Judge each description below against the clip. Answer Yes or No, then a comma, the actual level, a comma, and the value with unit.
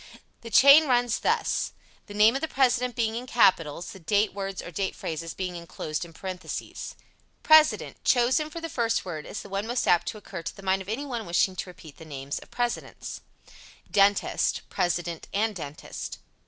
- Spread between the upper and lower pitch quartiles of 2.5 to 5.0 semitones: No, wide, 5.6 semitones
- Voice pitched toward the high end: Yes, high, 200 Hz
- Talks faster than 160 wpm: Yes, average, 190 wpm